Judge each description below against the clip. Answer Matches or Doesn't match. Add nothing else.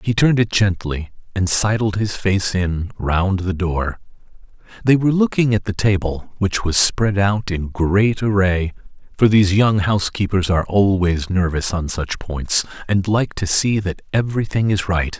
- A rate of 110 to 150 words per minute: Doesn't match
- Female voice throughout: Doesn't match